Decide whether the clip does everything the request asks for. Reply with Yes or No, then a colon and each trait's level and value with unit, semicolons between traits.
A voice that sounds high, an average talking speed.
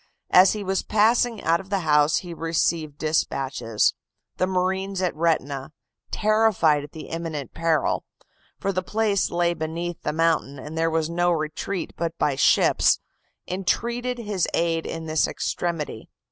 No: medium, 170 Hz; average, 150 wpm